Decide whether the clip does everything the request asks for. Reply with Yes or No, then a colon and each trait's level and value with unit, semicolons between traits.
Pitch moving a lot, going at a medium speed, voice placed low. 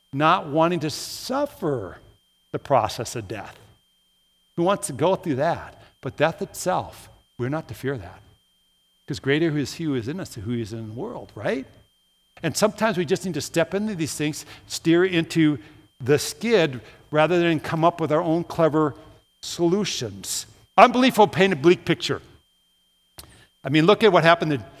No: wide, 6.2 semitones; average, 180 wpm; medium, 150 Hz